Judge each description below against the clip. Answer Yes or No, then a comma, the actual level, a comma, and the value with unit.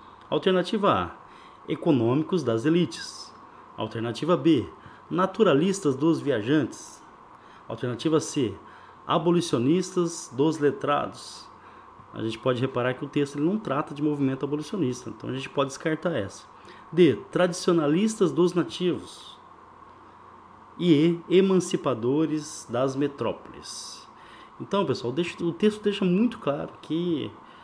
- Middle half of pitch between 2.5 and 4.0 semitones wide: No, average, 4.4 semitones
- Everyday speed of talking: No, slow, 110 wpm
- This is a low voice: No, medium, 165 Hz